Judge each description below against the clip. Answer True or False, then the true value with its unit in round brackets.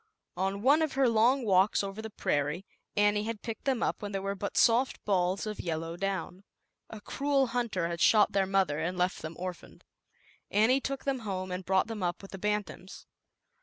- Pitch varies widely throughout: False (3.6 semitones)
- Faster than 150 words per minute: True (205 wpm)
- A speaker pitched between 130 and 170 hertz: False (200 Hz)